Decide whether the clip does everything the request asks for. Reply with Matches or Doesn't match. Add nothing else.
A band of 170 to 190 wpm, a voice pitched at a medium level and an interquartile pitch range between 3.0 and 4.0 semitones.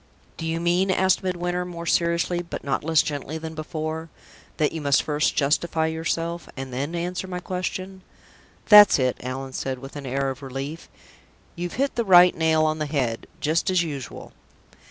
Matches